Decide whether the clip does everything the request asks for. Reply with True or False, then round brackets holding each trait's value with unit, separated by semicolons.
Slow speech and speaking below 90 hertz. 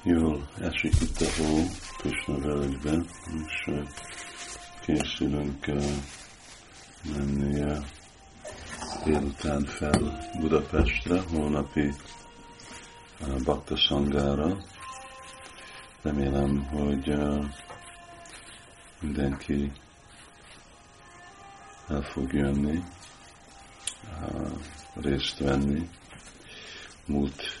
True (55 wpm; 75 Hz)